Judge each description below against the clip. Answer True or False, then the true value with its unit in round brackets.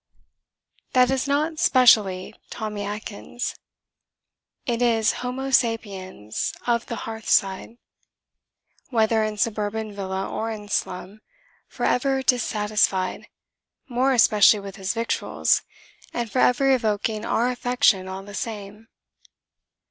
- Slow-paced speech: True (110 wpm)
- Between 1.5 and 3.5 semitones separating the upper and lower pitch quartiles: True (3.2 semitones)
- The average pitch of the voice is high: True (220 Hz)